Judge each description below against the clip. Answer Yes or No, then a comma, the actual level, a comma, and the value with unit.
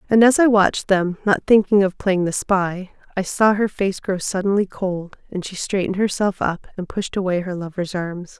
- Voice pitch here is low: No, high, 190 Hz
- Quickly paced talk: No, average, 195 wpm